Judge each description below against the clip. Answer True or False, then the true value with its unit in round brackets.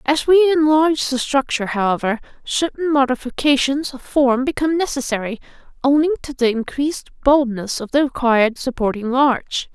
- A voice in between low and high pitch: False (270 Hz)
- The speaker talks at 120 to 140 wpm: True (135 wpm)